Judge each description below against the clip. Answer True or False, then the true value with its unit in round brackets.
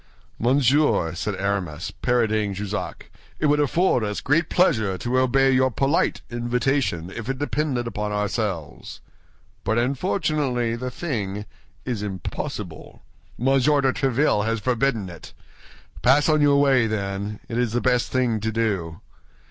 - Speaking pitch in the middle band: False (120 Hz)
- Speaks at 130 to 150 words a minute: True (135 wpm)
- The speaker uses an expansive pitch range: False (4.6 semitones)